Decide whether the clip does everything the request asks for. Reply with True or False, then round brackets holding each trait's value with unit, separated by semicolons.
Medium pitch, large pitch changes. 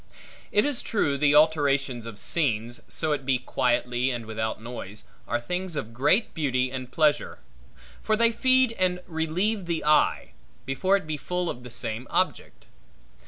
True (145 Hz; 6.5 semitones)